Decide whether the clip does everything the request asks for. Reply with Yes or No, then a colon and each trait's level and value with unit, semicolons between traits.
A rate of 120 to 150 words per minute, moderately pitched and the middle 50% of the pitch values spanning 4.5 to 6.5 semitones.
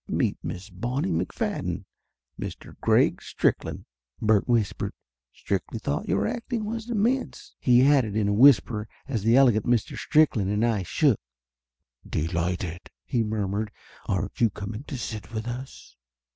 No: average, 145 wpm; low, 110 Hz; average, 5.1 semitones